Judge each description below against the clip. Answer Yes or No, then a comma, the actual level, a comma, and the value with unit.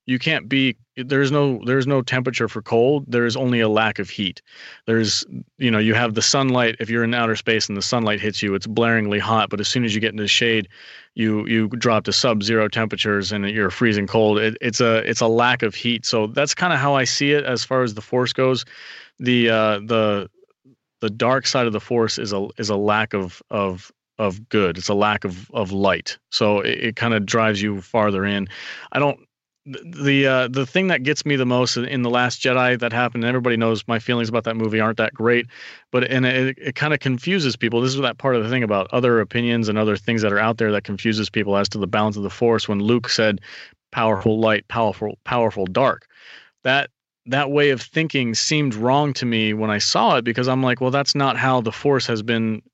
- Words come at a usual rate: No, fast, 235 wpm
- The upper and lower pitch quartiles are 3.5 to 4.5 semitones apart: No, average, 3.0 semitones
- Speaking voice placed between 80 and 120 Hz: Yes, low, 115 Hz